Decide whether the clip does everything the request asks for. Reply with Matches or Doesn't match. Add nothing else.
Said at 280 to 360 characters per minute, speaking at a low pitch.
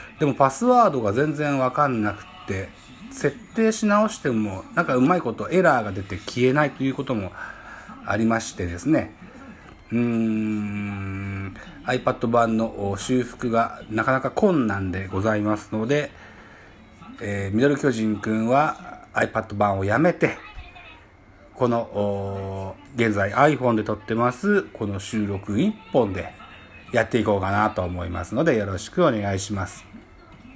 Matches